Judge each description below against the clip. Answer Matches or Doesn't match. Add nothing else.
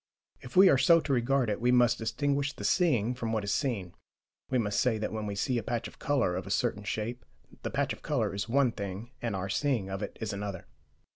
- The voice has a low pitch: Matches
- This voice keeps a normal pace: Doesn't match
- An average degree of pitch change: Matches